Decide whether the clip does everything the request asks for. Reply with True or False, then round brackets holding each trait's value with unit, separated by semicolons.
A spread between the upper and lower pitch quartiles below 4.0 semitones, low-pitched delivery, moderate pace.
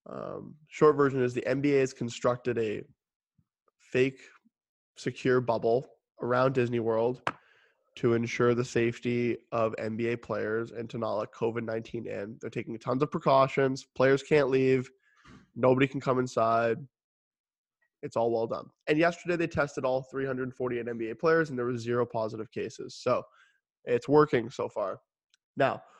True (2.6 semitones; 125 Hz; 150 wpm)